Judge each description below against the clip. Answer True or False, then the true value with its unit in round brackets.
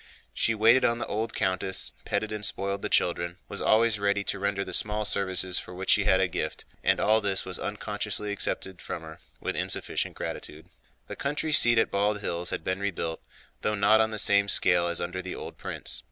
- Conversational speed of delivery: False (210 wpm)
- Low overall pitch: True (100 Hz)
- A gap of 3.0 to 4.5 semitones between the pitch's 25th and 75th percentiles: False (2.5 semitones)